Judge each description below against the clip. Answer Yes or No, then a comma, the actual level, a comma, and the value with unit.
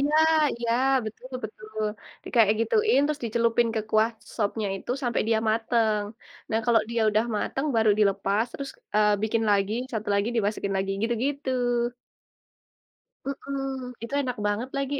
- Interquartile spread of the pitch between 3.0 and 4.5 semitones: No, narrow, 2.6 semitones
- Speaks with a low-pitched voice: No, high, 225 Hz